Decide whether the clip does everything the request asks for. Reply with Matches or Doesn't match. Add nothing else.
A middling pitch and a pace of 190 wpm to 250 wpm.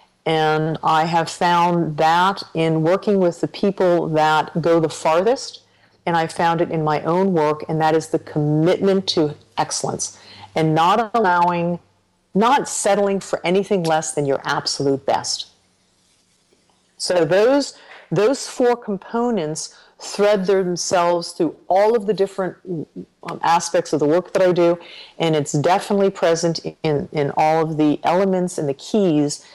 Doesn't match